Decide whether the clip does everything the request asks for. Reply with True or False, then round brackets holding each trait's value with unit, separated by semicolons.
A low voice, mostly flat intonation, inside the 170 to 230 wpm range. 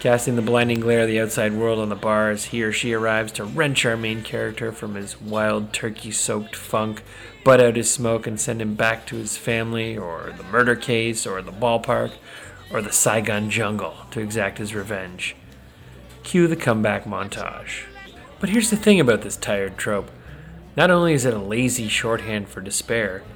True (110 Hz; 1.8 semitones; 190 wpm)